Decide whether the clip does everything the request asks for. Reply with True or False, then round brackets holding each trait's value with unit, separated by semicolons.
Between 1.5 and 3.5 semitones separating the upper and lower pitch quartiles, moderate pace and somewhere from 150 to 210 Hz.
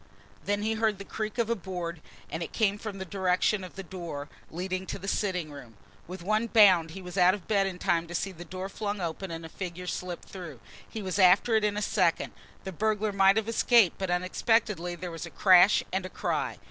False (2.9 semitones; 230 wpm; 190 Hz)